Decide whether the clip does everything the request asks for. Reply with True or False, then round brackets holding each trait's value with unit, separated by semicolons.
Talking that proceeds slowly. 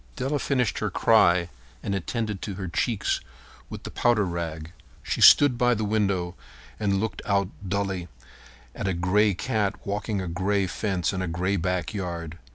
False (165 wpm)